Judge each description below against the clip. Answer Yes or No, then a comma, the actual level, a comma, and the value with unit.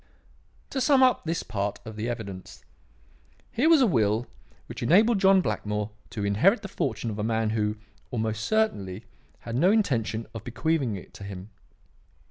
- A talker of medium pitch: No, low, 115 Hz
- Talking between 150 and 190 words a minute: Yes, average, 165 wpm